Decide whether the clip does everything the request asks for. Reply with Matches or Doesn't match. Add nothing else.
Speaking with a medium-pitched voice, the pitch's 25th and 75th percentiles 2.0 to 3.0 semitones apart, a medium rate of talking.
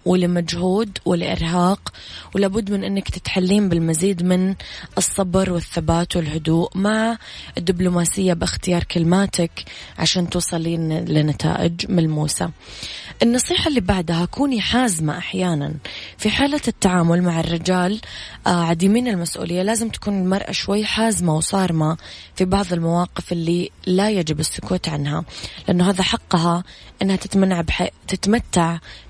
Doesn't match